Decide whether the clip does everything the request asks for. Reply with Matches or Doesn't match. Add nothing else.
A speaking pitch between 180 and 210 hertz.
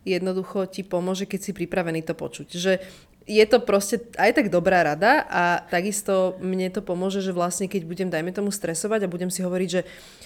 Matches